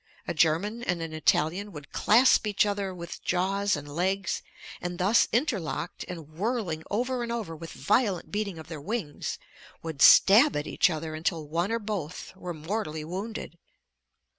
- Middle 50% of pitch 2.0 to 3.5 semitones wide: No, average, 4.7 semitones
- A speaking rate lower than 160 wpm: No, average, 165 wpm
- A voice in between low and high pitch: Yes, medium, 180 Hz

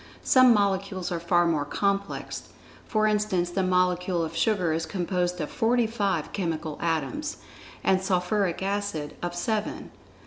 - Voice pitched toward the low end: No, medium, 185 Hz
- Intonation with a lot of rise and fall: No, average, 3.0 semitones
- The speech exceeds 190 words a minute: No, average, 140 wpm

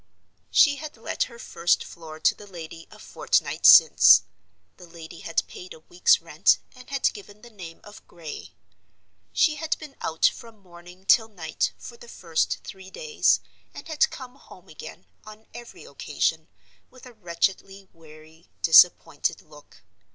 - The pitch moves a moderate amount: No, wide, 6.1 semitones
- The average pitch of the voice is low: No, high, 190 Hz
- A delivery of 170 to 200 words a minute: No, average, 160 wpm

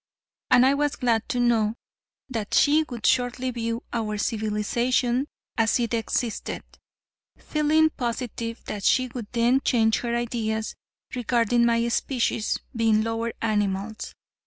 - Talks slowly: Yes, slow, 130 wpm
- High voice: Yes, high, 235 Hz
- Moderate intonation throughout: No, narrow, 2.0 semitones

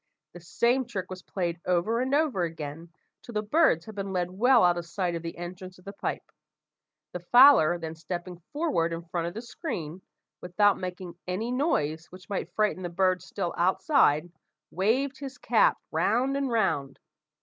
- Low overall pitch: No, medium, 185 Hz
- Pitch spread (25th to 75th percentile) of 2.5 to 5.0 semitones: No, wide, 5.5 semitones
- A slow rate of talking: No, average, 180 wpm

